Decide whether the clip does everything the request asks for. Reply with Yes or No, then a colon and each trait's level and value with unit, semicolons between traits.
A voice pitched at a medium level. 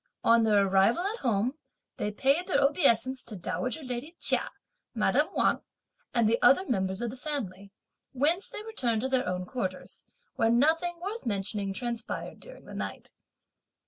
No: high, 240 Hz